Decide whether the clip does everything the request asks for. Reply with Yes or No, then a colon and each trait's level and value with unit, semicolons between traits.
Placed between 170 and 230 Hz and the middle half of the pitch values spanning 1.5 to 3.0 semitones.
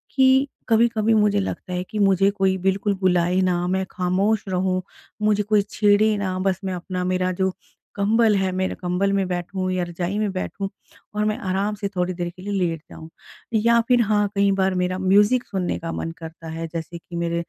Yes: high, 190 Hz; narrow, 2.4 semitones